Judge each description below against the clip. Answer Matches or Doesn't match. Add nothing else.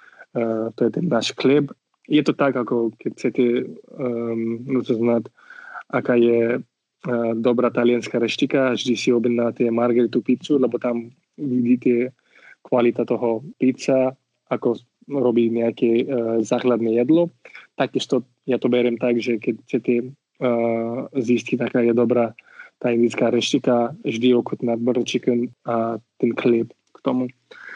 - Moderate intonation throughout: Doesn't match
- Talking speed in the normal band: Matches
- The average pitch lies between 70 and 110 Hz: Doesn't match